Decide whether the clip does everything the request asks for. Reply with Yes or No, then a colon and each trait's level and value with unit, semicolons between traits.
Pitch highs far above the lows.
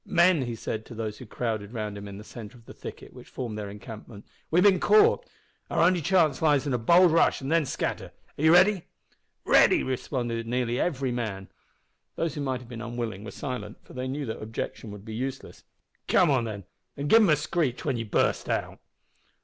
Yes: wide, 5.8 semitones